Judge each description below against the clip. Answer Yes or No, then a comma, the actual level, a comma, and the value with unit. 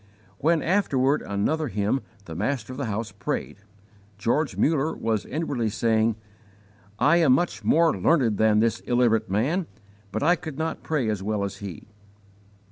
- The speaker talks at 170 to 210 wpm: No, average, 155 wpm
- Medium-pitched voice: No, low, 125 Hz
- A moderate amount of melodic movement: No, wide, 6.5 semitones